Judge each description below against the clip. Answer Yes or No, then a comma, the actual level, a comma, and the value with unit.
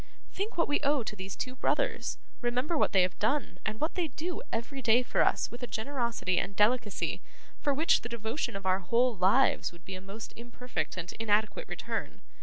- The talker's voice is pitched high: Yes, high, 235 Hz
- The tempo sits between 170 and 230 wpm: Yes, fast, 205 wpm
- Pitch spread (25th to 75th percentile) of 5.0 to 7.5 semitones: Yes, wide, 5.6 semitones